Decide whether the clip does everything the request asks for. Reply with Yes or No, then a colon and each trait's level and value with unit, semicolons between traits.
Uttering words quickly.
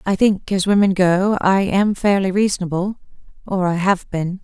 No: average, 160 wpm